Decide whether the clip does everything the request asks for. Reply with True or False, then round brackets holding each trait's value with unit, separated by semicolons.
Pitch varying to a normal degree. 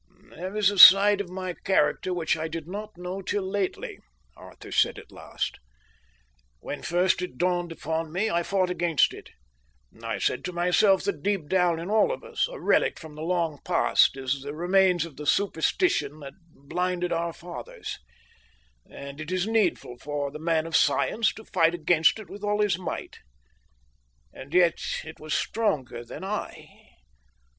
True (3.3 semitones)